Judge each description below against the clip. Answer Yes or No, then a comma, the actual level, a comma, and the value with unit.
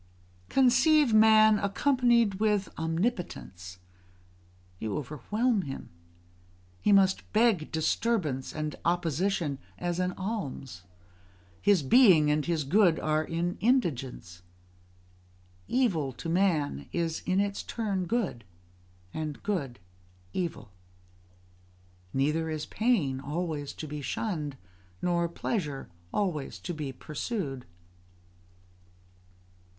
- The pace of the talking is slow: Yes, slow, 100 wpm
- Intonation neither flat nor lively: No, wide, 5.9 semitones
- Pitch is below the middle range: No, medium, 170 Hz